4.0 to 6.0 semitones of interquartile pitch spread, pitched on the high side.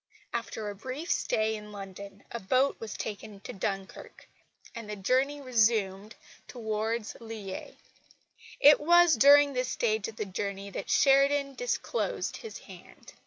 Yes: average, 5.0 semitones; high, 225 Hz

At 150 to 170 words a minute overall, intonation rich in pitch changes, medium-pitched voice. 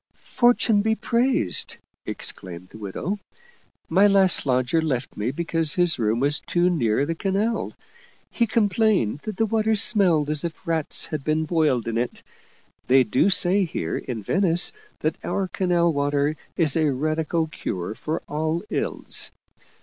Yes: average, 160 wpm; wide, 6.1 semitones; medium, 160 Hz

